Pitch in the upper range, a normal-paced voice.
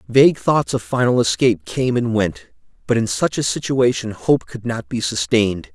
No: low, 120 Hz; average, 190 wpm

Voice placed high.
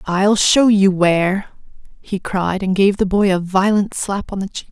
Yes: high, 195 Hz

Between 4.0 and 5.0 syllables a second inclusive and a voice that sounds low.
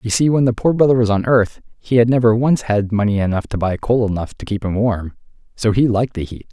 No: 6.0 syllables/s; low, 110 Hz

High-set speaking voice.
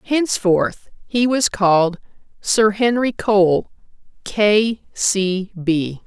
Yes: high, 205 Hz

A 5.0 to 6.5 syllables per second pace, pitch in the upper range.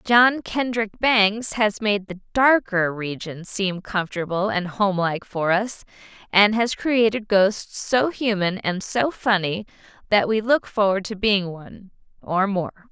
No: 4.1 syllables/s; high, 205 Hz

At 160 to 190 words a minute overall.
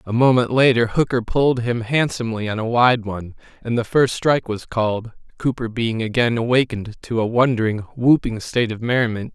Yes: average, 180 wpm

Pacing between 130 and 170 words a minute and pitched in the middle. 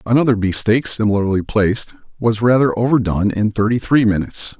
No: average, 155 wpm; low, 110 Hz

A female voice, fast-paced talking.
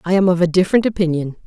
Yes: female; fast, 245 wpm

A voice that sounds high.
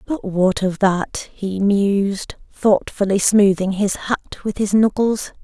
Yes: high, 200 Hz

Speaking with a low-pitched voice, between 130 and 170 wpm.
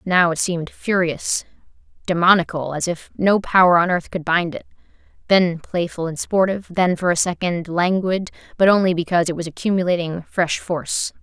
No: medium, 175 Hz; average, 165 wpm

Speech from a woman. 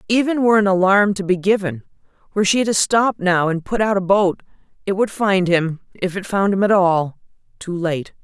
Yes: female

